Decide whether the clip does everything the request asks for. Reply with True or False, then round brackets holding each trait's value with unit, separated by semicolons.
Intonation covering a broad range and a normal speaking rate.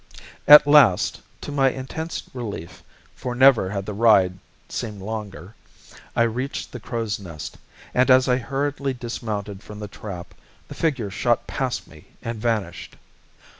False (4.5 semitones; 145 wpm)